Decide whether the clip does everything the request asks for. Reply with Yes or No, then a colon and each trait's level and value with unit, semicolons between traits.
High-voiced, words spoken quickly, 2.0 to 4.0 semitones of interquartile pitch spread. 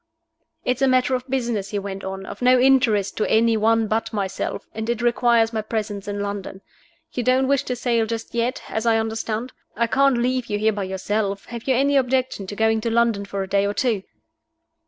Yes: high, 225 Hz; fast, 215 wpm; average, 3.3 semitones